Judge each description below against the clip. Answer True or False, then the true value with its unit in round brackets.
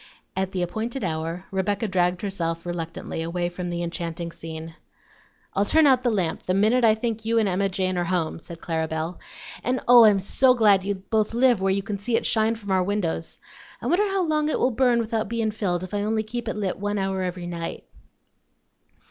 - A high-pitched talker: True (195 Hz)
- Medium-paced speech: False (215 wpm)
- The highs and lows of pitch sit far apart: False (4.2 semitones)